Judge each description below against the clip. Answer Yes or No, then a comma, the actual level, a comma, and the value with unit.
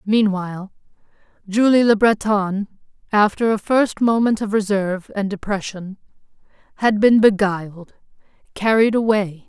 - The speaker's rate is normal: No, slow, 110 wpm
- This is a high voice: Yes, high, 205 Hz